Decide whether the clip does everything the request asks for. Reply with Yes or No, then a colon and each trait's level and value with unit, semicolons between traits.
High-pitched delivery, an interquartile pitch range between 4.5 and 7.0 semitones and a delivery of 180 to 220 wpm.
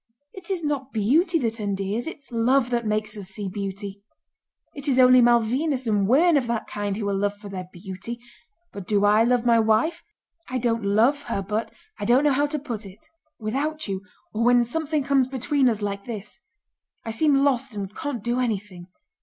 Yes: high, 230 Hz; average, 4.8 semitones; average, 195 wpm